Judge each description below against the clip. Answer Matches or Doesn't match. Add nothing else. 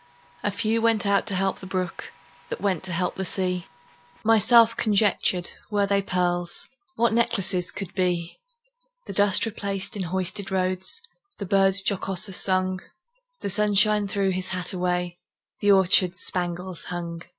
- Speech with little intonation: Matches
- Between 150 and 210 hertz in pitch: Matches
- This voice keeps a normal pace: Matches